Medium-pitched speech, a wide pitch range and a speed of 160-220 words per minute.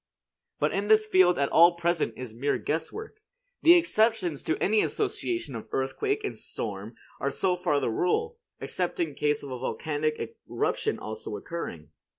Yes: medium, 170 Hz; wide, 7.8 semitones; average, 165 wpm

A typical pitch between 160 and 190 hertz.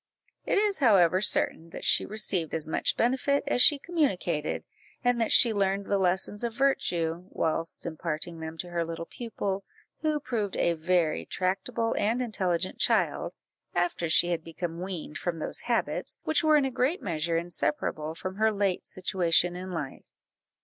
Yes: medium, 185 Hz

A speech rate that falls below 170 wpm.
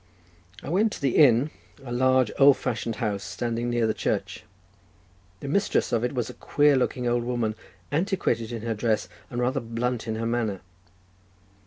No: average, 175 wpm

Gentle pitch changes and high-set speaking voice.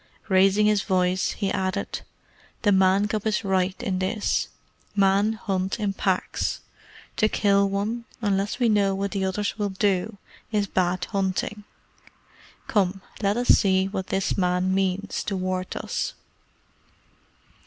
Yes: narrow, 1.6 semitones; high, 195 Hz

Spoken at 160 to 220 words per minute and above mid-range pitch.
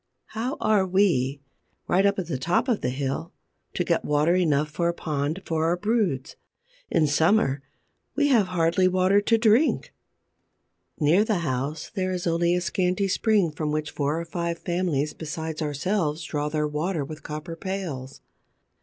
No: average, 165 wpm; medium, 170 Hz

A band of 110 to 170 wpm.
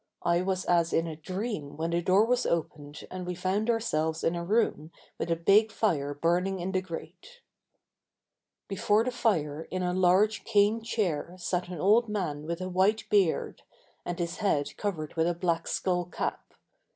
No: average, 180 wpm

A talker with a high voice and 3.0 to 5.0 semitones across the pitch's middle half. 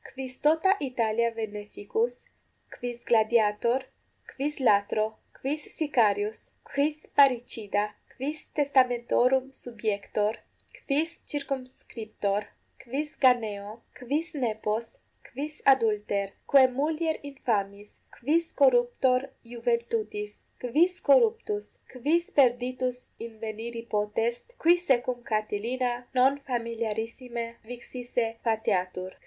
Yes: high, 240 Hz; average, 3.9 semitones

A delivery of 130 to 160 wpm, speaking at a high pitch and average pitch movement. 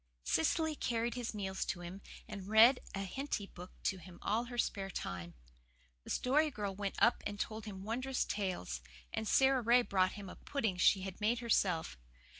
No: average, 185 wpm; high, 210 Hz; average, 4.1 semitones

